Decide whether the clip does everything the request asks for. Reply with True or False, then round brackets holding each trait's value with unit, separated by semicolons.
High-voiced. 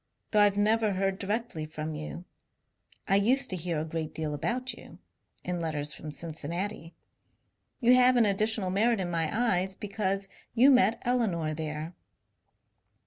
True (195 Hz)